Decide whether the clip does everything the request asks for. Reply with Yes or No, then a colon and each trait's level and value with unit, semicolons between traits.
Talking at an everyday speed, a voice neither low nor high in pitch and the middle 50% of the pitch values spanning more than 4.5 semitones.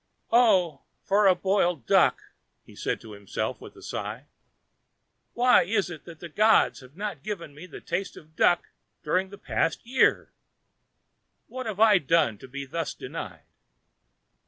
Yes: average, 160 wpm; medium, 180 Hz; average, 5.2 semitones